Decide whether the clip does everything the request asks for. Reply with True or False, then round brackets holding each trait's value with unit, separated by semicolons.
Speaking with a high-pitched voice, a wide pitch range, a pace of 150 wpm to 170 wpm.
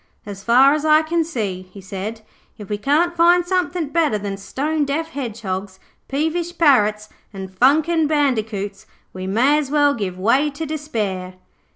True (265 Hz; 7.4 semitones; 160 wpm)